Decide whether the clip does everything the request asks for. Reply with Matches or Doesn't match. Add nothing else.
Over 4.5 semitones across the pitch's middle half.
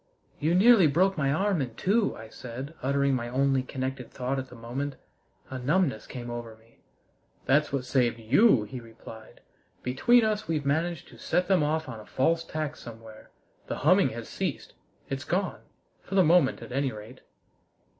Matches